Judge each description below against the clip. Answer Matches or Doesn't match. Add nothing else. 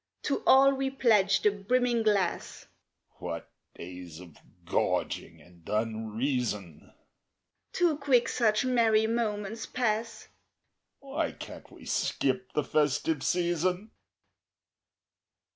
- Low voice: Doesn't match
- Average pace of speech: Doesn't match